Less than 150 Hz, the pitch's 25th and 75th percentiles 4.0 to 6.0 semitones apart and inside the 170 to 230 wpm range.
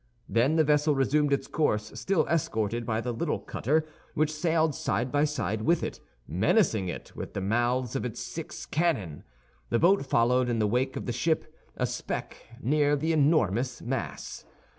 Yes: low, 135 Hz; average, 4.9 semitones; average, 175 wpm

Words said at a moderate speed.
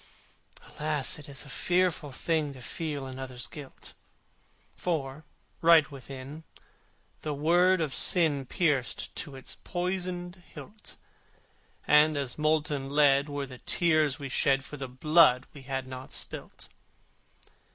No: slow, 130 wpm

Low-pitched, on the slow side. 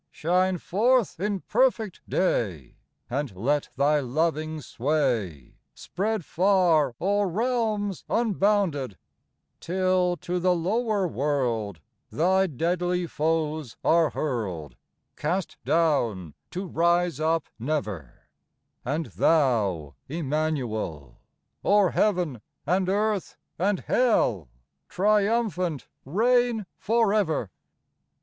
No: medium, 165 Hz; slow, 95 wpm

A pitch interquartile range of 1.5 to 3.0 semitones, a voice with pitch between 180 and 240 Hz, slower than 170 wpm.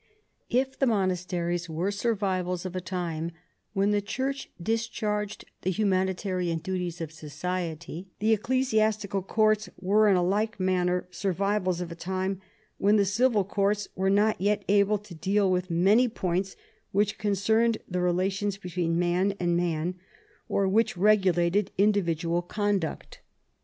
Yes: average, 2.7 semitones; high, 190 Hz; average, 140 wpm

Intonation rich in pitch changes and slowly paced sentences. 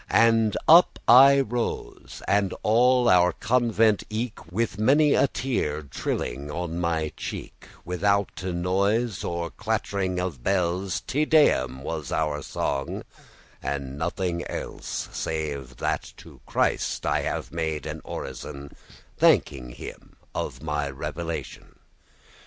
Yes: wide, 6.6 semitones; slow, 120 wpm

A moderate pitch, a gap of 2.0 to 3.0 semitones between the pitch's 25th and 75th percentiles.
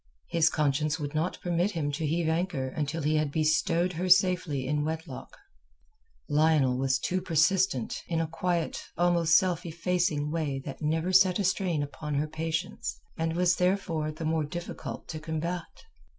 Yes: medium, 160 Hz; narrow, 2.6 semitones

